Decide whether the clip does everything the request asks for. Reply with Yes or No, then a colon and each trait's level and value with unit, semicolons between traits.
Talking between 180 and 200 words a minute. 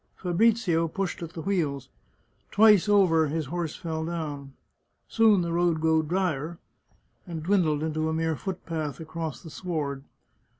No: average, 145 wpm